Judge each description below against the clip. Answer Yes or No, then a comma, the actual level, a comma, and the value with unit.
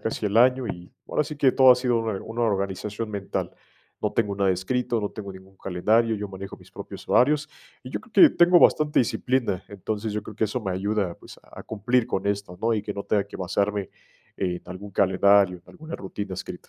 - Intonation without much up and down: No, average, 3.6 semitones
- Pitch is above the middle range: No, low, 105 Hz